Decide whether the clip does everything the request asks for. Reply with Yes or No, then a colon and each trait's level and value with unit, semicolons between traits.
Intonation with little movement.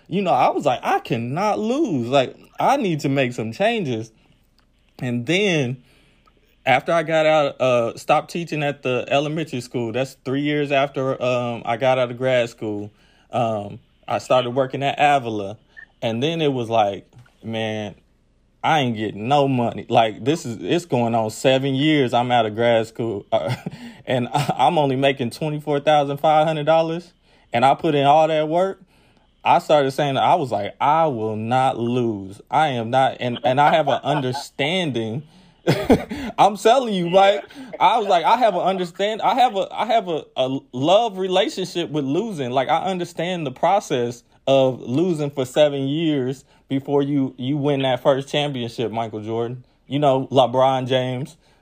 No: average, 4.3 semitones